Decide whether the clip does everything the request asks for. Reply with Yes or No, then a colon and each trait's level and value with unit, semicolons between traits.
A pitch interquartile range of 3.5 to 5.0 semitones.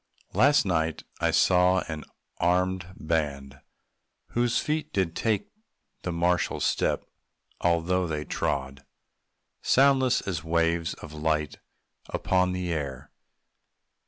No: average, 2.9 semitones